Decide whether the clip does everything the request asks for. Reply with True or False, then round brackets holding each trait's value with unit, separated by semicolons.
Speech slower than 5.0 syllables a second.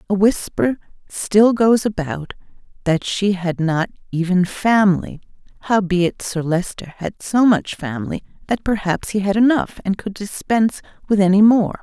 True (4.7 syllables/s)